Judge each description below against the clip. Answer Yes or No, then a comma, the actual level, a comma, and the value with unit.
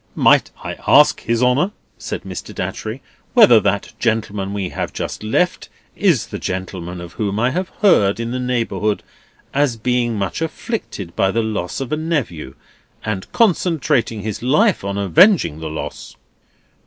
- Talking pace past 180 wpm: No, average, 155 wpm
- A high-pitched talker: No, low, 115 Hz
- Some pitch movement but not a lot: No, wide, 6.8 semitones